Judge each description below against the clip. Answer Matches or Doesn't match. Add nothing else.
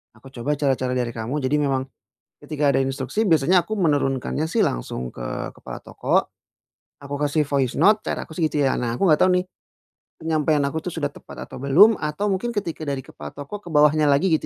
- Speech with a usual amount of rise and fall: Matches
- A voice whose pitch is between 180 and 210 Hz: Doesn't match